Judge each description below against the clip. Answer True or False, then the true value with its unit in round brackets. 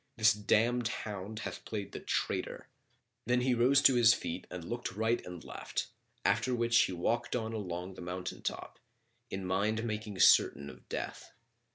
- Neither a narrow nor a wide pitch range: True (4.1 semitones)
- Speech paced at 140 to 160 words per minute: False (170 wpm)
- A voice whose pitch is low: True (110 Hz)